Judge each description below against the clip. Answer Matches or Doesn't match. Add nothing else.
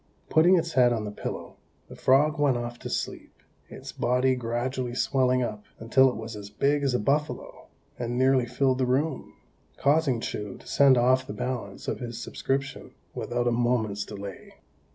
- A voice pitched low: Matches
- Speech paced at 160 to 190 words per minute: Matches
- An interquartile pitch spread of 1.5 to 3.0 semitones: Matches